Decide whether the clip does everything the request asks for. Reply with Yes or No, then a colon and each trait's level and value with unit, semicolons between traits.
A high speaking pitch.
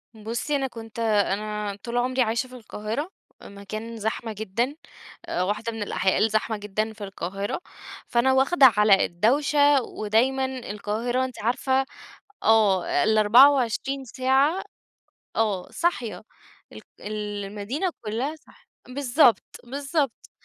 Yes: high, 230 Hz